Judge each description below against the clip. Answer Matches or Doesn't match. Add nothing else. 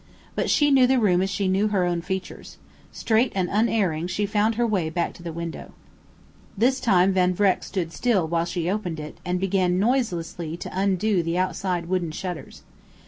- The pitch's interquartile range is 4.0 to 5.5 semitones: Doesn't match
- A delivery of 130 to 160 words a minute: Doesn't match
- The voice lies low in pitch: Doesn't match